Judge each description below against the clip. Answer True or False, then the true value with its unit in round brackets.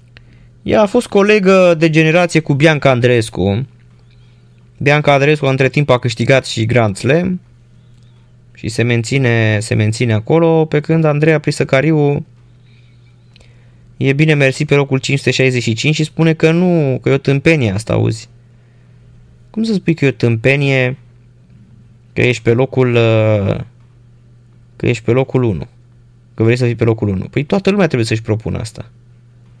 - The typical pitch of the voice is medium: False (120 Hz)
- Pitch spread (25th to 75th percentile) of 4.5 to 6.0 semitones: False (3.3 semitones)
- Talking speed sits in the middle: True (150 wpm)